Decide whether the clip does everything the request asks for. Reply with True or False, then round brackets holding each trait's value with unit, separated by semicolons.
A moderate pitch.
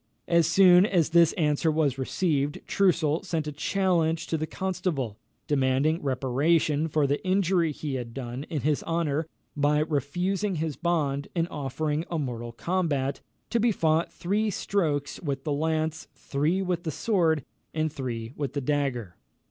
True (155 Hz)